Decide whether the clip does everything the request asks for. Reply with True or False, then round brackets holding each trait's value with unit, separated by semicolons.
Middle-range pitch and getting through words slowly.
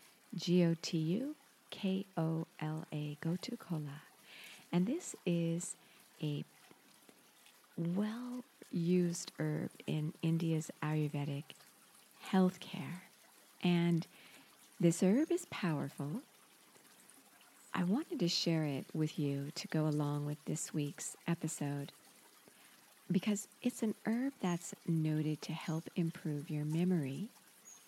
True (170 Hz; 110 wpm)